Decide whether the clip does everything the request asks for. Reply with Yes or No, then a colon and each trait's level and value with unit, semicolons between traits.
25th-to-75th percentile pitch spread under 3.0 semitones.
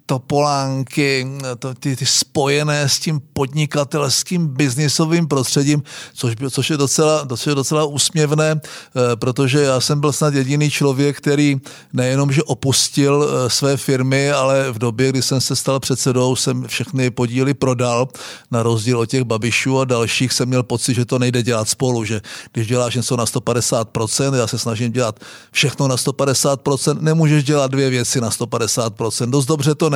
Yes: narrow, 2.6 semitones